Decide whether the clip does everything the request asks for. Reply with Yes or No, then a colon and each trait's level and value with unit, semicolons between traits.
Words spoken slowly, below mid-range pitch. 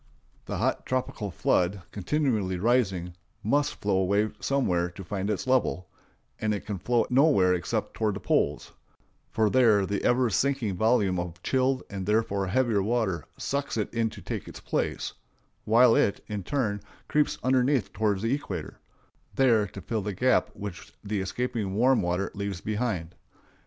No: average, 160 wpm; low, 105 Hz